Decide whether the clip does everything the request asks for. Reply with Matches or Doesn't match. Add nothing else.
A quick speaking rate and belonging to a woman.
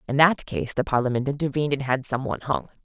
Matches